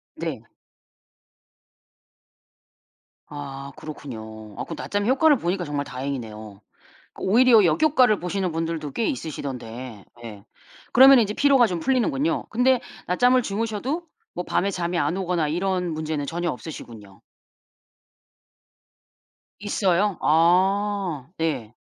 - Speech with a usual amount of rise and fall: No, wide, 7.2 semitones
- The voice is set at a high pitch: No, medium, 175 Hz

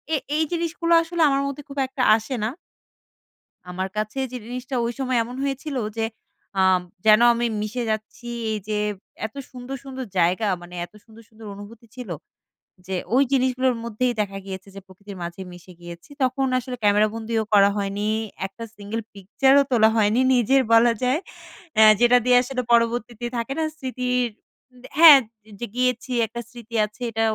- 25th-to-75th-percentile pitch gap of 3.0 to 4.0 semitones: Yes, average, 3.5 semitones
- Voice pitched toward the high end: Yes, high, 235 Hz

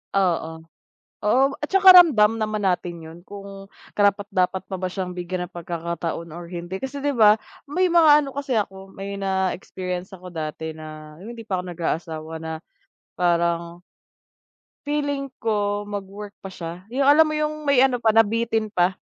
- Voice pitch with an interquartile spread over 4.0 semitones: Yes, average, 4.7 semitones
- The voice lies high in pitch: Yes, high, 195 Hz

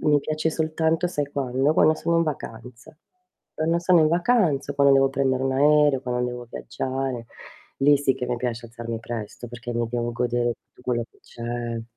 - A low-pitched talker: Yes, low, 130 Hz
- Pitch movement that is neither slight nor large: Yes, average, 3.9 semitones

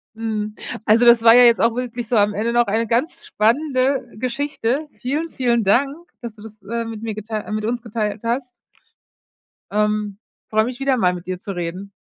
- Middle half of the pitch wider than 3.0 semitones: No, narrow, 2.6 semitones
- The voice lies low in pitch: No, high, 230 Hz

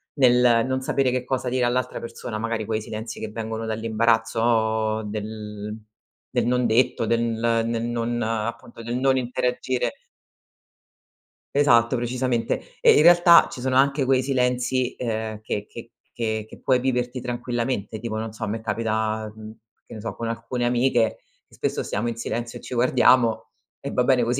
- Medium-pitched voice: No, low, 115 Hz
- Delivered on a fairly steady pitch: Yes, narrow, 2.2 semitones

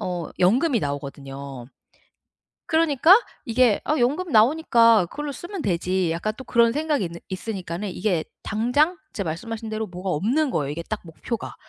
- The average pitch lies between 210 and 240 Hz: Yes, high, 215 Hz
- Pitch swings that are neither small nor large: No, wide, 7.3 semitones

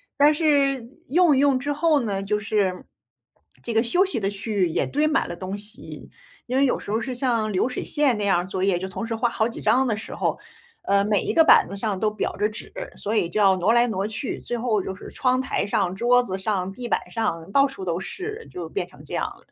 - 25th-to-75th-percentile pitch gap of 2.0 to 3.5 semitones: No, average, 4.9 semitones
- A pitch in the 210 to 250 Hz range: Yes, high, 220 Hz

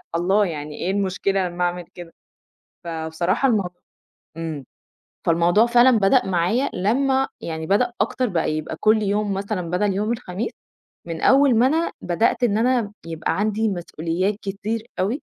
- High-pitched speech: Yes, high, 195 Hz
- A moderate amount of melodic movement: Yes, average, 4.8 semitones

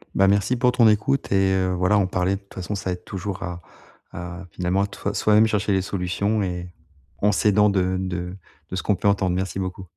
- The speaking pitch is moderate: No, very low, 95 Hz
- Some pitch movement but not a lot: No, narrow, 2.0 semitones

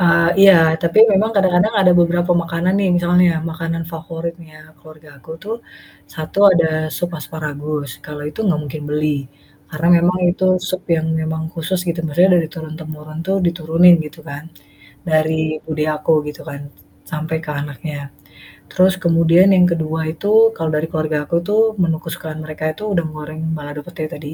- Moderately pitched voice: Yes, medium, 165 Hz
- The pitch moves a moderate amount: No, narrow, 2.2 semitones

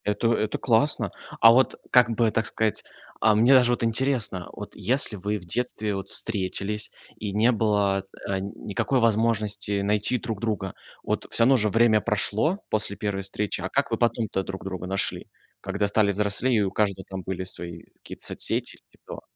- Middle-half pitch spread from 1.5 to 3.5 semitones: Yes, average, 2.8 semitones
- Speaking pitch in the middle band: No, low, 105 Hz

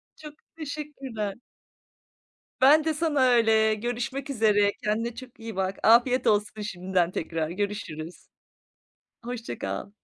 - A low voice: No, high, 225 Hz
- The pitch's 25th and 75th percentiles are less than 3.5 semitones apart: No, average, 4.3 semitones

